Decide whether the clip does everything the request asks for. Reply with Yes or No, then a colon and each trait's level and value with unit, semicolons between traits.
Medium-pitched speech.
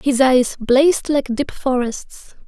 No: very high, 265 Hz